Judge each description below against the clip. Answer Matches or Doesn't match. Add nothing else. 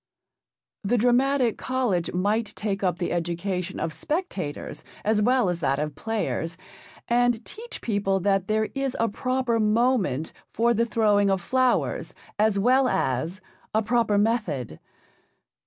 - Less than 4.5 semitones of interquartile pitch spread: Doesn't match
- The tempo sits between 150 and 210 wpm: Doesn't match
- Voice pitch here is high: Matches